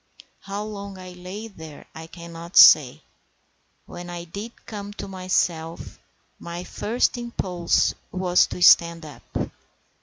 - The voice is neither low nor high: Yes, medium, 180 Hz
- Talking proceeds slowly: Yes, slow, 125 wpm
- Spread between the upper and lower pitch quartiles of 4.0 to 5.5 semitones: No, average, 2.9 semitones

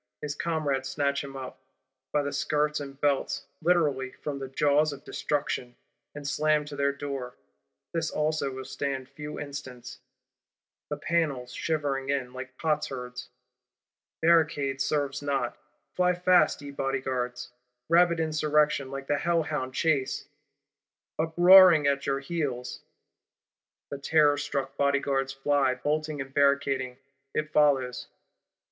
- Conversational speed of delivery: No, slow, 125 wpm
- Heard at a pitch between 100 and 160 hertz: Yes, medium, 140 Hz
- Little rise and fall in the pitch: Yes, narrow, 2.1 semitones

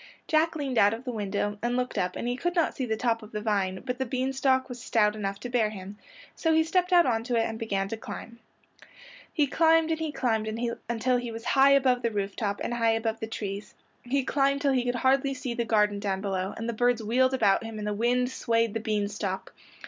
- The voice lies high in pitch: Yes, high, 235 Hz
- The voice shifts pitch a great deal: No, average, 3.7 semitones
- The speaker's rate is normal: No, fast, 245 wpm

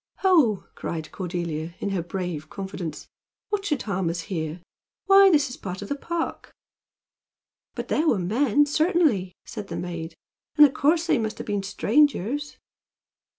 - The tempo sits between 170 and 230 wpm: No, average, 160 wpm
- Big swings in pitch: Yes, wide, 8.8 semitones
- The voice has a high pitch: Yes, high, 205 Hz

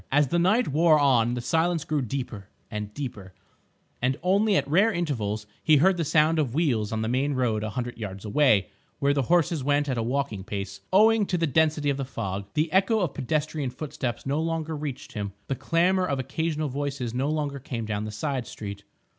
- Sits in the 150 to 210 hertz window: No, medium, 140 Hz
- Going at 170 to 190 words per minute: No, fast, 205 wpm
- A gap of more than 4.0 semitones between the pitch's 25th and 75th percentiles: Yes, wide, 5.4 semitones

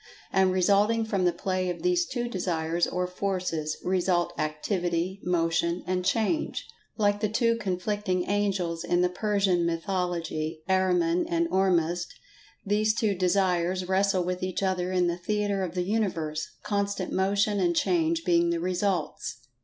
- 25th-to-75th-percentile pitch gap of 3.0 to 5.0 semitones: No, narrow, 2.6 semitones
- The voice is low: No, medium, 185 Hz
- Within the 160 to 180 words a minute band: No, average, 140 wpm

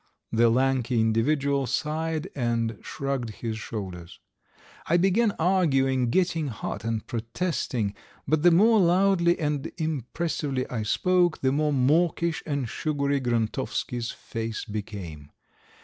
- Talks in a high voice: No, low, 135 Hz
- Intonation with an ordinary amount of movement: No, wide, 6.1 semitones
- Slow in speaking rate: Yes, slow, 115 wpm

